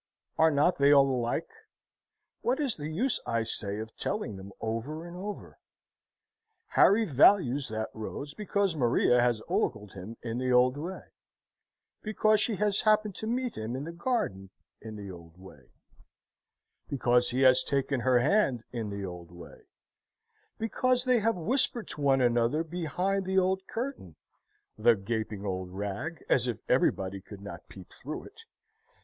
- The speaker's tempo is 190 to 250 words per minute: No, average, 160 wpm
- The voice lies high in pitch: No, low, 135 Hz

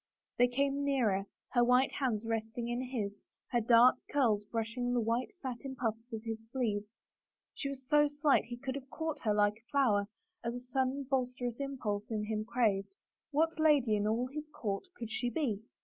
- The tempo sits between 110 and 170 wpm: No, average, 185 wpm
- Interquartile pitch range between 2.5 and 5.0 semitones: Yes, average, 3.4 semitones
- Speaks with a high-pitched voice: Yes, high, 245 Hz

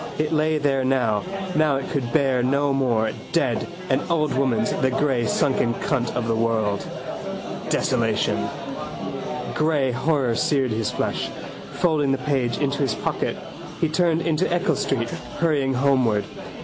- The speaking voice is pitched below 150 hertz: Yes, low, 135 Hz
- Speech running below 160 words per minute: Yes, average, 145 wpm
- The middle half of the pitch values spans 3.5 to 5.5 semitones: Yes, average, 3.9 semitones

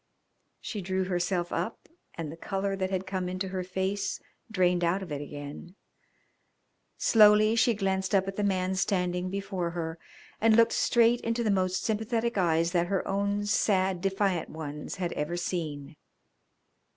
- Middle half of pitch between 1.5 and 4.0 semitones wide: Yes, narrow, 2.5 semitones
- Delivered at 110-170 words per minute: Yes, average, 160 wpm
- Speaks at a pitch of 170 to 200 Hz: Yes, high, 190 Hz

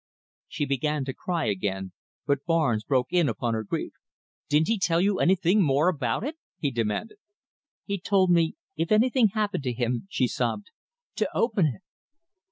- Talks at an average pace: Yes, average, 170 wpm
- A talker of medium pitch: Yes, medium, 155 Hz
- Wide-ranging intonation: Yes, wide, 7.5 semitones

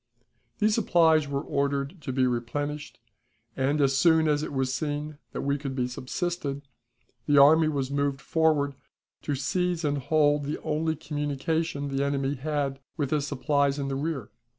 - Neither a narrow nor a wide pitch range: No, narrow, 2.0 semitones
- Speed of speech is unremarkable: Yes, average, 165 wpm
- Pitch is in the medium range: Yes, medium, 145 Hz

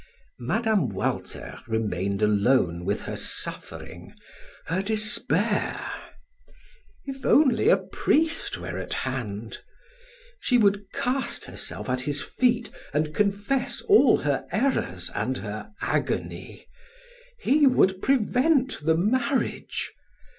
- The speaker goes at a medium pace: No, slow, 105 wpm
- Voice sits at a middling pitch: No, high, 200 Hz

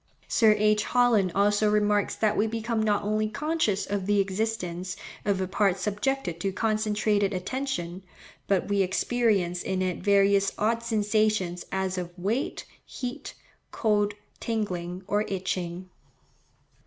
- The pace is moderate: No, slow, 130 wpm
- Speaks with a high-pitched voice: Yes, high, 205 Hz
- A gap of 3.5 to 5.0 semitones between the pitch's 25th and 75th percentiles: No, narrow, 2.4 semitones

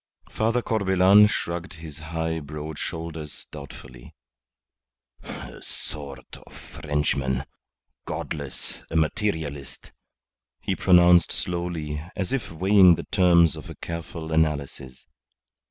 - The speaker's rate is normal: No, slow, 105 wpm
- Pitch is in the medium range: No, very low, 80 Hz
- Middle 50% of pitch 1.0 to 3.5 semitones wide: Yes, average, 3.2 semitones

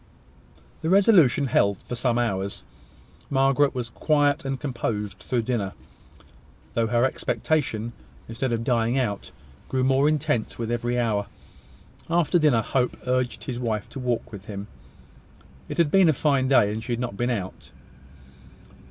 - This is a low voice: Yes, low, 125 Hz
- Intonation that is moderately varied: Yes, average, 3.2 semitones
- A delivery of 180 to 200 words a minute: No, average, 150 wpm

